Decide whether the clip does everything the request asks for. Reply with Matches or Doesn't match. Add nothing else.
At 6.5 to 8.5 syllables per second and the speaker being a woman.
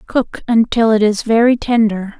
Doesn't match